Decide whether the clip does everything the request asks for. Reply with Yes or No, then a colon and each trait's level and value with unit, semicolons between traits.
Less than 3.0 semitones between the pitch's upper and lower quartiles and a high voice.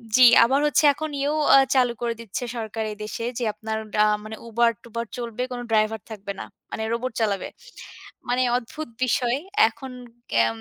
Yes: narrow, 2.4 semitones; high, 235 Hz